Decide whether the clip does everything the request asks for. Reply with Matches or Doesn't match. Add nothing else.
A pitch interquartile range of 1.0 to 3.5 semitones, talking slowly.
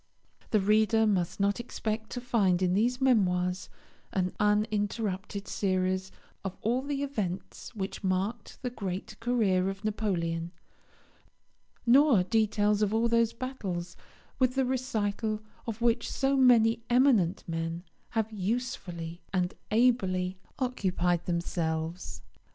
Doesn't match